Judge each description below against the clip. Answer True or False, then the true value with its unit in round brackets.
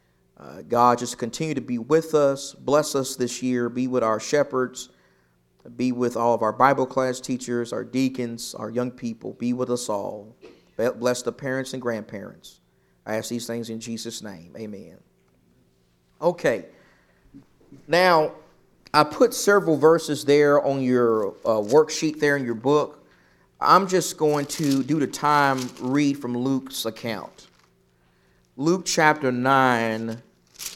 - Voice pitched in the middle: False (125 Hz)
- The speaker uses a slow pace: False (145 wpm)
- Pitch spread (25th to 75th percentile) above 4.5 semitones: False (3.7 semitones)